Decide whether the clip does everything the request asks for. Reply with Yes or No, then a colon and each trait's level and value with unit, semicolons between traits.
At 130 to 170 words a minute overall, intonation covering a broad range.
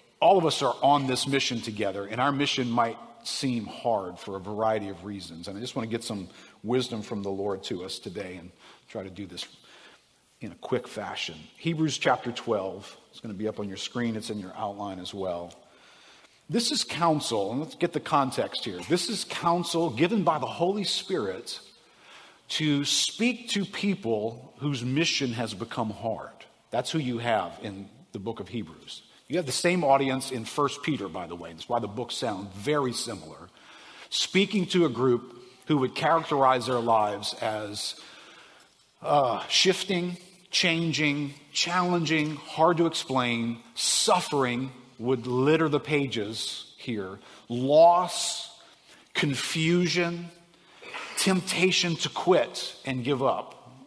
Yes: average, 160 wpm; wide, 7.3 semitones